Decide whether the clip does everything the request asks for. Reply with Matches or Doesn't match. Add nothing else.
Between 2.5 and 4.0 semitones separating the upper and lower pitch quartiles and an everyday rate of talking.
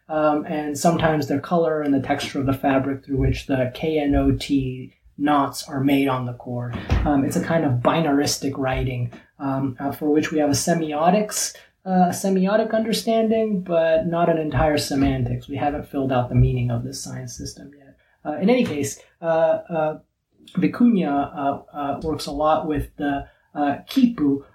Matches